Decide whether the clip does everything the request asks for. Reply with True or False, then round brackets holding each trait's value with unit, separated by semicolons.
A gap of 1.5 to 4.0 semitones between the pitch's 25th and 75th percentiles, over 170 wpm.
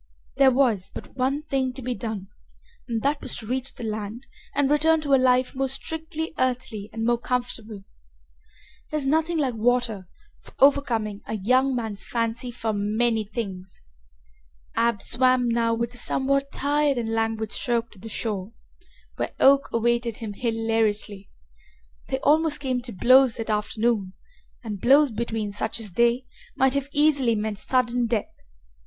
False (3.3 semitones; 160 wpm)